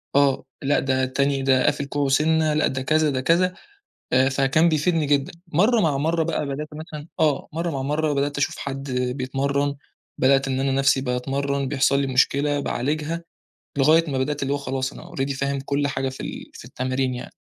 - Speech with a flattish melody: Yes, narrow, 2.2 semitones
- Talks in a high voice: No, medium, 140 Hz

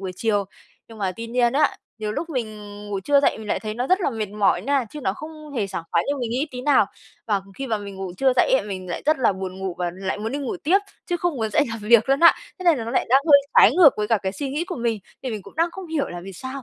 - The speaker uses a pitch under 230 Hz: No, high, 235 Hz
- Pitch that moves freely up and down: Yes, wide, 5.7 semitones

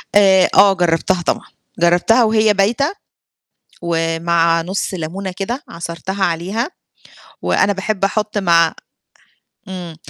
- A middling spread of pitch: Yes, average, 3.3 semitones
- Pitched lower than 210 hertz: Yes, high, 190 Hz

